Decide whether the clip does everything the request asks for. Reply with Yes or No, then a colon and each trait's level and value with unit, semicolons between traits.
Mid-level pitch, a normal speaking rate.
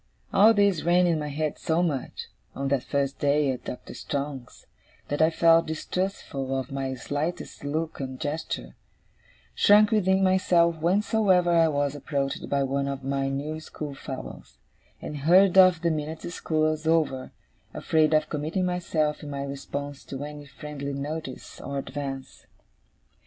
Yes: medium, 150 Hz; average, 150 wpm